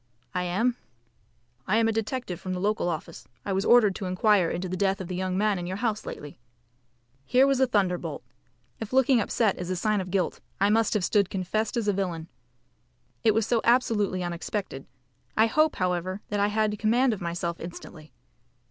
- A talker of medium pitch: No, high, 200 Hz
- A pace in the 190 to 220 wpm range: Yes, average, 195 wpm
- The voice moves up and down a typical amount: Yes, average, 3.6 semitones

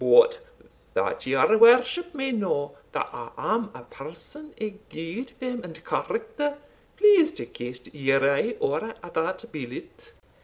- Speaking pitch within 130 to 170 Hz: No, high, 225 Hz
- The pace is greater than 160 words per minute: No, average, 140 wpm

